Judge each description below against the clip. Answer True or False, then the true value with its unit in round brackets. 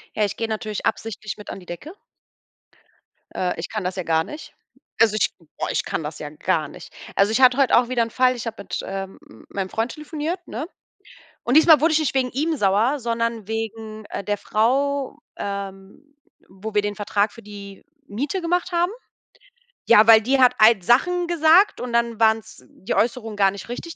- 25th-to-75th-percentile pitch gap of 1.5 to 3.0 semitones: False (5.1 semitones)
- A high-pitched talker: True (225 Hz)